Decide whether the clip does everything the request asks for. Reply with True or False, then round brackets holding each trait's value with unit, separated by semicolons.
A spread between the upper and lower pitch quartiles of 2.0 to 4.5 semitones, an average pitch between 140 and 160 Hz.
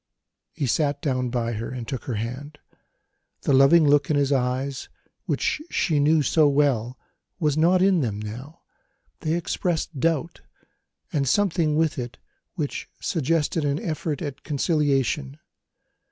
True (3.5 semitones; 145 Hz)